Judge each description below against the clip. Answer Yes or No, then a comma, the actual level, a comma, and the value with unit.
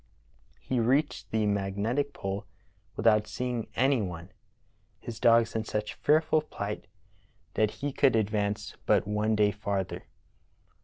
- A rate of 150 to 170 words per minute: No, slow, 135 wpm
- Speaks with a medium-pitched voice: No, low, 110 Hz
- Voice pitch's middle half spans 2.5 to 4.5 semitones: Yes, average, 3.3 semitones